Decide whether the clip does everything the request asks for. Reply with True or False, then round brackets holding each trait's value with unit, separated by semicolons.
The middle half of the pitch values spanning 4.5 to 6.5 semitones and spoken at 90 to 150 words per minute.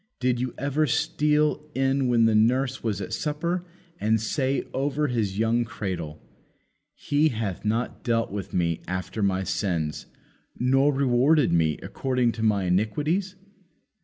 True (5.2 semitones; 140 wpm)